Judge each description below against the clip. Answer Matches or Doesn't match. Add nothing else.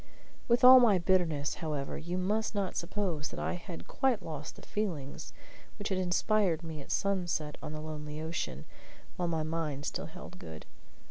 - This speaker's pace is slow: Doesn't match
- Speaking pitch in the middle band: Matches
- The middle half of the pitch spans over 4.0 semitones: Matches